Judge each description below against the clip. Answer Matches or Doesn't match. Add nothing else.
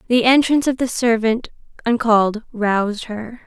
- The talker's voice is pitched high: Matches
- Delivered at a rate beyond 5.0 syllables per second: Doesn't match